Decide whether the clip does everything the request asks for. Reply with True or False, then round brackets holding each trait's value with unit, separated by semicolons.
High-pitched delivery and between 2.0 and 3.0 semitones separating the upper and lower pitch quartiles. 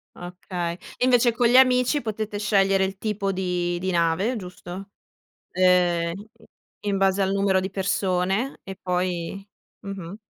True (195 Hz; 2.4 semitones)